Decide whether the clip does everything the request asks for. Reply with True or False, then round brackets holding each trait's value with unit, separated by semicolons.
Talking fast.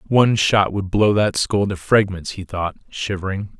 False (185 wpm)